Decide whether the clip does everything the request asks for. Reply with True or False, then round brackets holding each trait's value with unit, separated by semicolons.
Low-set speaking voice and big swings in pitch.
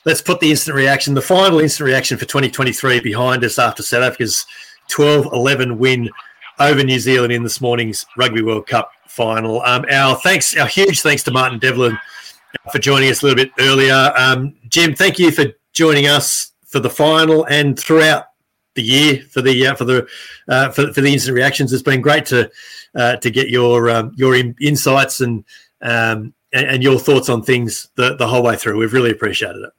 False (130 Hz; 2.7 semitones)